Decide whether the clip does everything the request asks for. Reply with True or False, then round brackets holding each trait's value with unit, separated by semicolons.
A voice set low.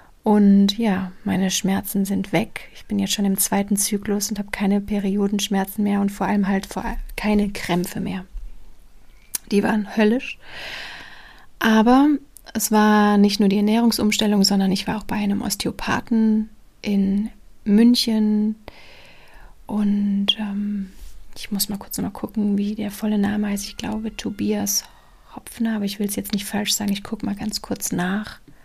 False (205 Hz)